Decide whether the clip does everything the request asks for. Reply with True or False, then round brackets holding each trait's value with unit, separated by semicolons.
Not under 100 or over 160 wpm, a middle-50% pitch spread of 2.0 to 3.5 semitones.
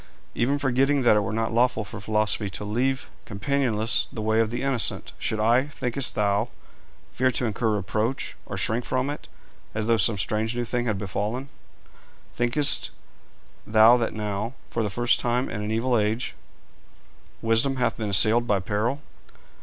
False (170 wpm; 2.6 semitones)